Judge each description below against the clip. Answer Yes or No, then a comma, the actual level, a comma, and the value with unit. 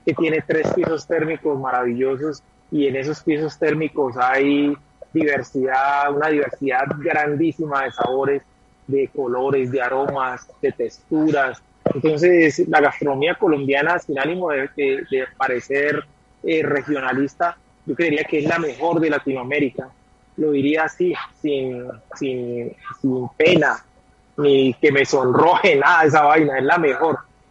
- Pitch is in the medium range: Yes, medium, 145 Hz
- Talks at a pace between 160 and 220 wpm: No, average, 135 wpm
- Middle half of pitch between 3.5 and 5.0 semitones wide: No, average, 3.0 semitones